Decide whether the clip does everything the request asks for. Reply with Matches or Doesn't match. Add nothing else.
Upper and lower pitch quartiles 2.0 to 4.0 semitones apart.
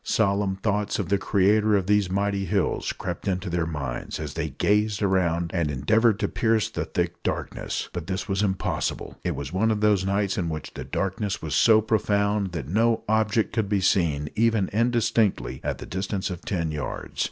Matches